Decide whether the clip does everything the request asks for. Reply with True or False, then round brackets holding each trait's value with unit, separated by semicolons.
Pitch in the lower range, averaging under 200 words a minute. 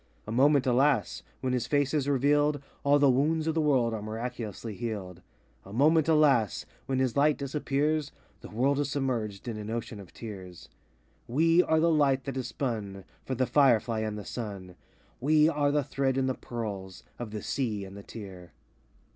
True (130 Hz; 185 wpm)